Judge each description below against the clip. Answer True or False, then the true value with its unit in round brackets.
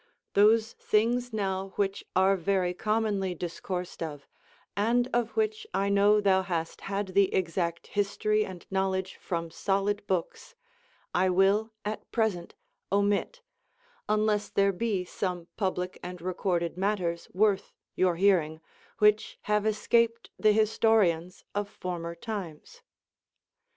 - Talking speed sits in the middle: False (125 wpm)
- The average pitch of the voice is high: True (195 Hz)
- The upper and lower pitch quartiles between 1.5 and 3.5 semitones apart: True (2.8 semitones)